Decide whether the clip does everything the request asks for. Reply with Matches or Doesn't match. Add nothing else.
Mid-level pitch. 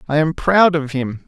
Matches